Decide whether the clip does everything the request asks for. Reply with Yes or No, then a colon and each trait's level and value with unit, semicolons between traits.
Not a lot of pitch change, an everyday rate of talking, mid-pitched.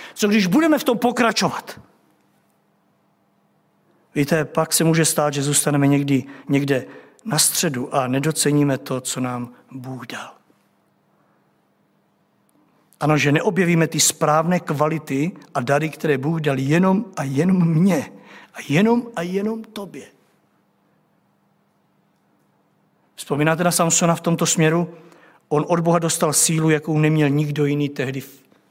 No: average, 3.2 semitones; average, 130 wpm; medium, 155 Hz